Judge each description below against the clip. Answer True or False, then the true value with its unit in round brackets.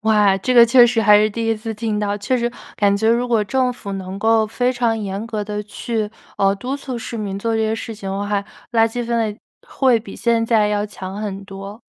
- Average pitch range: False (2.3 semitones)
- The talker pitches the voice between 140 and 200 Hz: False (220 Hz)